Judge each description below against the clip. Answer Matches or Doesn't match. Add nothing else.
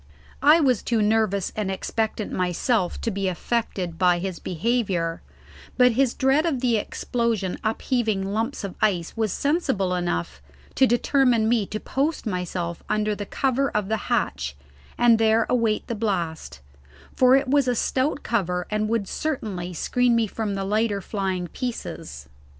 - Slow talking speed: Doesn't match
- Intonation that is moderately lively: Matches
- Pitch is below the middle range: Doesn't match